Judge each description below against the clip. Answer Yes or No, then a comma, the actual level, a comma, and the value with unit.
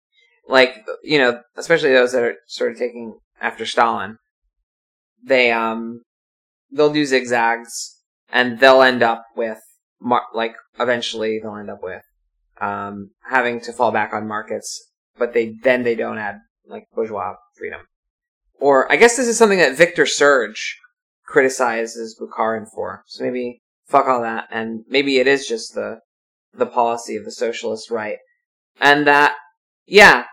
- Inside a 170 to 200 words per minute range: No, average, 150 wpm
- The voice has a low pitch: Yes, low, 125 Hz